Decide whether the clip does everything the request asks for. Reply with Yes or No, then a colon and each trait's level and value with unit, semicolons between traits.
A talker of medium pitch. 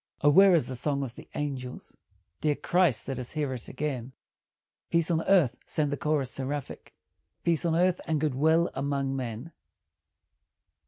Yes: medium, 145 Hz